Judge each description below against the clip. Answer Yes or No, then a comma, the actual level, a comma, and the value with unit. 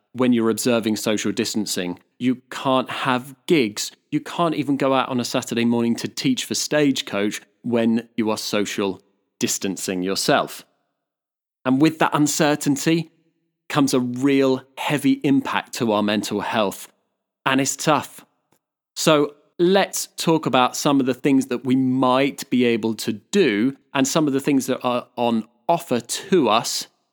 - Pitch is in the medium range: No, low, 130 Hz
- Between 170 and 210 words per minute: No, average, 155 wpm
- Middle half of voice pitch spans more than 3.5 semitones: Yes, average, 3.9 semitones